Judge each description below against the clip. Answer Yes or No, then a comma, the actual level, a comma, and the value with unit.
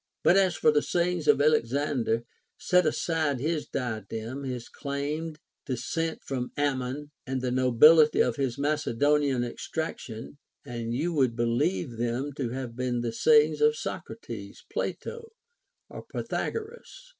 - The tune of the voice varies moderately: Yes, average, 4.4 semitones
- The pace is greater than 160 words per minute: No, slow, 135 wpm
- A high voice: No, medium, 140 Hz